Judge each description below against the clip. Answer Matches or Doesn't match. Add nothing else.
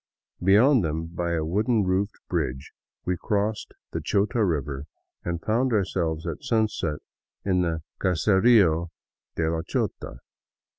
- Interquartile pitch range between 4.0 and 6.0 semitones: Matches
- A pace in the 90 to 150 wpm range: Matches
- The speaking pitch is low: Matches